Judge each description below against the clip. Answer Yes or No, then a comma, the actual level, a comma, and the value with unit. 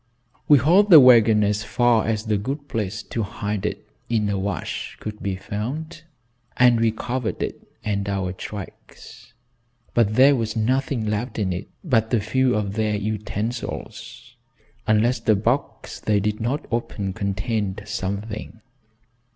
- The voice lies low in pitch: Yes, low, 110 Hz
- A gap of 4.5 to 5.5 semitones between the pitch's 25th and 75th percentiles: No, average, 2.9 semitones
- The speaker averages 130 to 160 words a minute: Yes, average, 150 wpm